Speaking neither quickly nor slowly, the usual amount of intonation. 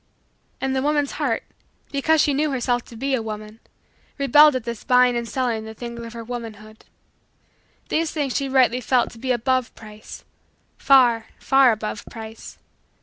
Yes: average, 165 wpm; average, 3.1 semitones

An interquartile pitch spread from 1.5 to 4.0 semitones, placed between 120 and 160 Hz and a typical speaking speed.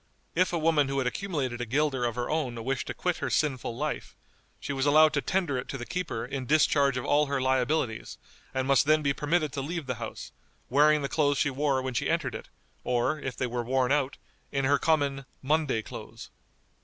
No: average, 2.9 semitones; medium, 140 Hz; fast, 215 wpm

